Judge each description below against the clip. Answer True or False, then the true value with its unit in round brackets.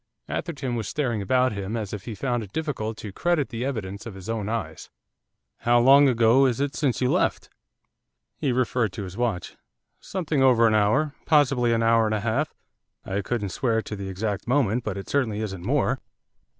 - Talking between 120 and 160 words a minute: False (195 wpm)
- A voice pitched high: False (115 Hz)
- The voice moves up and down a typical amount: True (4.0 semitones)